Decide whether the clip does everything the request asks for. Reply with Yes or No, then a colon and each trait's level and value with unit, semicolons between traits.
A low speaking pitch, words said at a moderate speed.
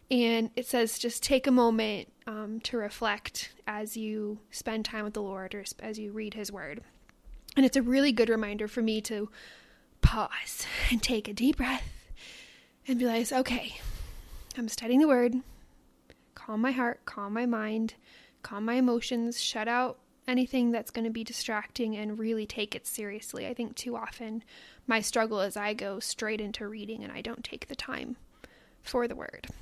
No: high, 225 Hz; average, 180 wpm